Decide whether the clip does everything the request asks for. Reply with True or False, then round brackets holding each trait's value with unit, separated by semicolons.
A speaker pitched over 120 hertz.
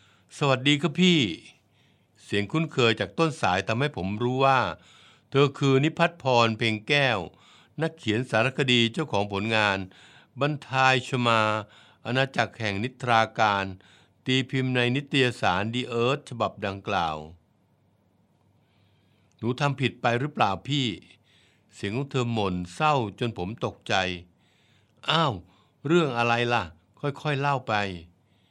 False (115 Hz)